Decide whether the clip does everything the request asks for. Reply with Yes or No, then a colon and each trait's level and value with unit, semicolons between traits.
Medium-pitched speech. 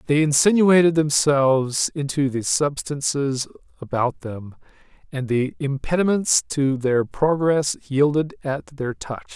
Yes: medium, 145 Hz